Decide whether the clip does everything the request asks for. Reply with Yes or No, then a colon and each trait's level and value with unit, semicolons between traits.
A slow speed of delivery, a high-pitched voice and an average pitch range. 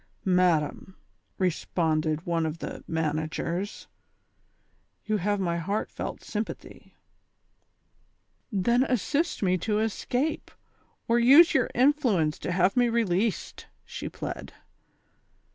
No: slow, 100 wpm; high, 195 Hz; wide, 5.7 semitones